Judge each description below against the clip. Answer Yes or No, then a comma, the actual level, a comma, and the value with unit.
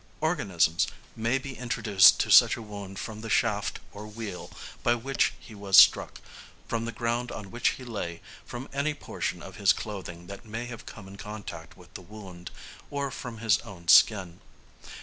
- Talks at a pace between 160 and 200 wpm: Yes, average, 180 wpm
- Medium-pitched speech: No, low, 110 Hz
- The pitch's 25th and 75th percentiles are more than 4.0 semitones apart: No, average, 3.5 semitones